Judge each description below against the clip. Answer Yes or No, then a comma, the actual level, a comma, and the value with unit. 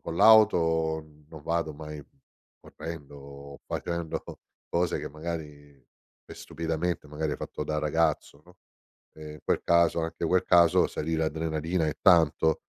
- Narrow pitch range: Yes, narrow, 1.8 semitones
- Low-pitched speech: Yes, very low, 80 Hz